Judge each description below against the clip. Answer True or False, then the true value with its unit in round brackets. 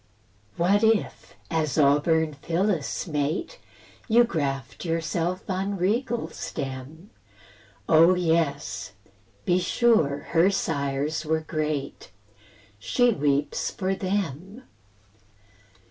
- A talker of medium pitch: True (165 Hz)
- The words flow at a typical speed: False (90 wpm)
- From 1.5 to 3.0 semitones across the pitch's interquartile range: False (4.8 semitones)